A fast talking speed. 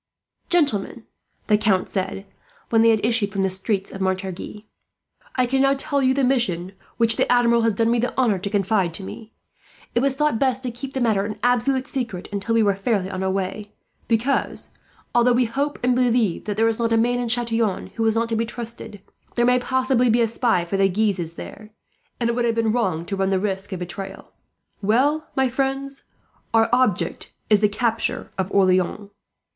Yes: fast, 210 wpm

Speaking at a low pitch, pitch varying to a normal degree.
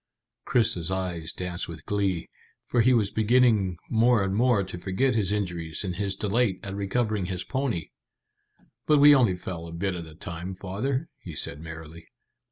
Yes: very low, 95 Hz; average, 4.7 semitones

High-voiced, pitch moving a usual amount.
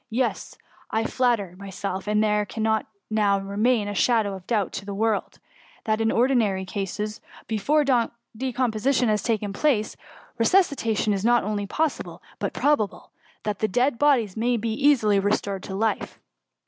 Yes: high, 220 Hz; average, 3.0 semitones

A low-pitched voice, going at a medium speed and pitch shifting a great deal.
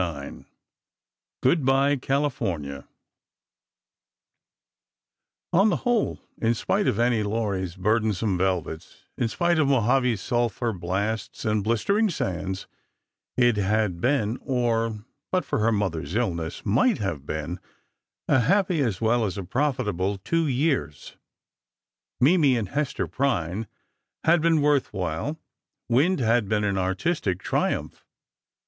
No: low, 115 Hz; slow, 115 wpm; wide, 6.4 semitones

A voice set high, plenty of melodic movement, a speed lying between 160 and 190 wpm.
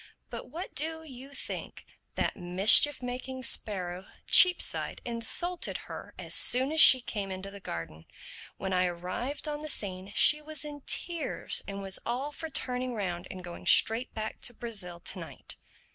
Yes: high, 240 Hz; wide, 7.5 semitones; average, 165 wpm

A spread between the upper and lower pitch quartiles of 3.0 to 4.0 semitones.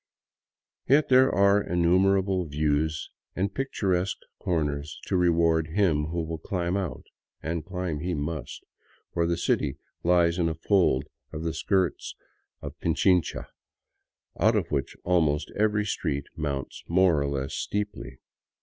Yes: average, 3.6 semitones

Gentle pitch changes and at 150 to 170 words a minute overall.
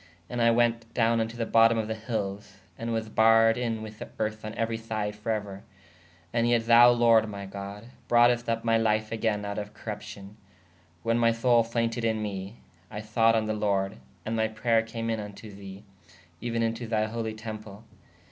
No: narrow, 1.4 semitones; average, 195 wpm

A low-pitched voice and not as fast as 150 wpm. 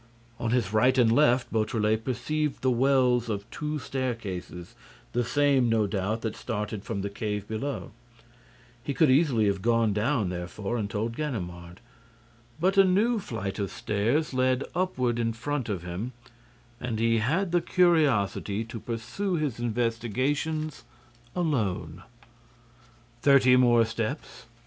Yes: low, 120 Hz; average, 140 wpm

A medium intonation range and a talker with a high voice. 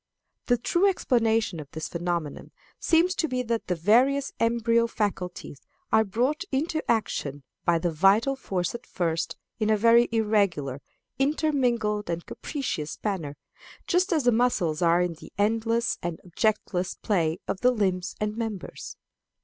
No: wide, 5.7 semitones; high, 215 Hz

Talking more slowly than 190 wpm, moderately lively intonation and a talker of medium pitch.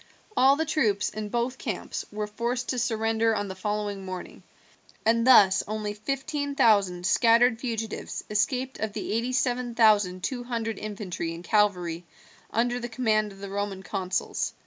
No: average, 160 wpm; average, 3.2 semitones; high, 220 Hz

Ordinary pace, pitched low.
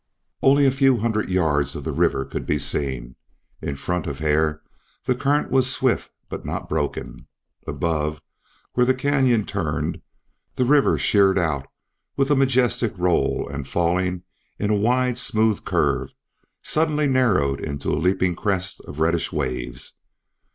Yes: average, 150 wpm; very low, 95 Hz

